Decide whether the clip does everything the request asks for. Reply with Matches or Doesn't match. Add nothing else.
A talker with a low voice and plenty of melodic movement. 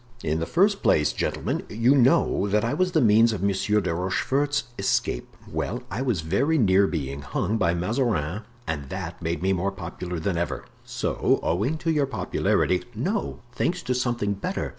Matches